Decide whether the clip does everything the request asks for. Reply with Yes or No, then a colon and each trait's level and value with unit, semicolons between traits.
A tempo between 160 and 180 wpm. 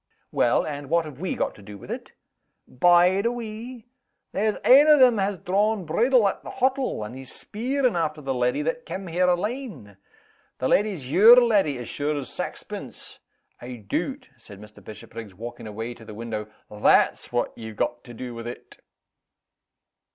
Yes: average, 175 wpm